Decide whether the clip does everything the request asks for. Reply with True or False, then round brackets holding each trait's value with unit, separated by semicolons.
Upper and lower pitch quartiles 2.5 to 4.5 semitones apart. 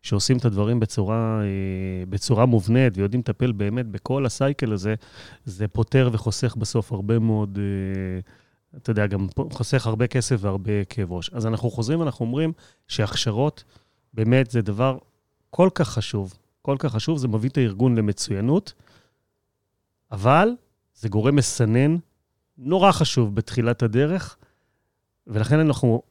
True (3.9 semitones)